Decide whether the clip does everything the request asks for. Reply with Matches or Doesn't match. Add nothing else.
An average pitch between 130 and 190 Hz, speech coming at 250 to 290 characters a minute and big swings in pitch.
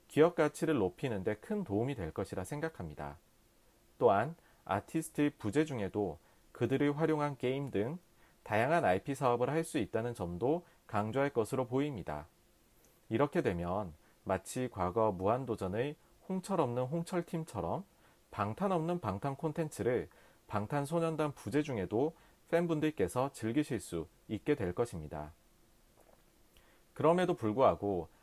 Matches